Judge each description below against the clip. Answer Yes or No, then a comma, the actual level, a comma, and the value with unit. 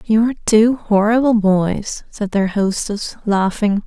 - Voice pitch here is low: No, high, 210 Hz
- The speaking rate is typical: No, slow, 125 wpm